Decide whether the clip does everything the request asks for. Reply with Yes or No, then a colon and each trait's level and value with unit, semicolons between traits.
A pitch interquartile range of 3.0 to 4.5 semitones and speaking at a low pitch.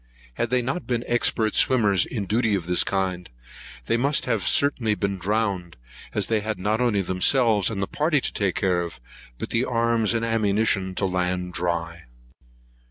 Yes: average, 4.1 semitones; low, 105 Hz